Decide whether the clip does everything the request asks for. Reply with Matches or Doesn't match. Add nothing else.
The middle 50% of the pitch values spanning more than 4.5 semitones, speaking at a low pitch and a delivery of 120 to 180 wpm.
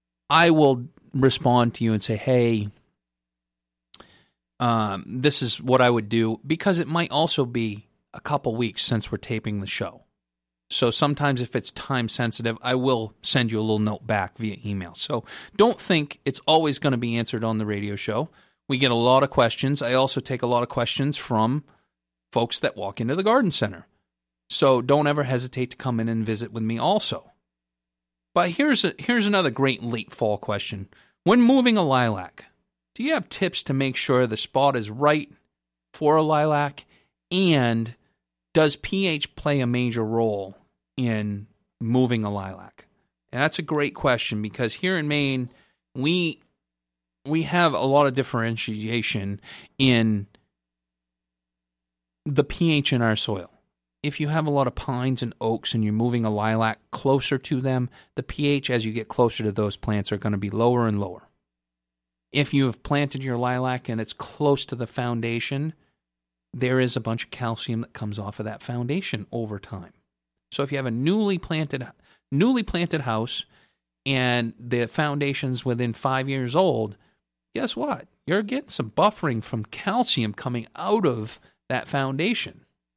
Matches